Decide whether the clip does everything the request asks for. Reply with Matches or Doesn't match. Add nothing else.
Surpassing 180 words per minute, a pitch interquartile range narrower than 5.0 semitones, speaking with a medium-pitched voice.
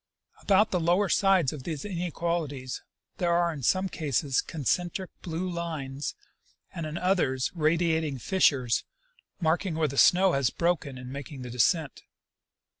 Doesn't match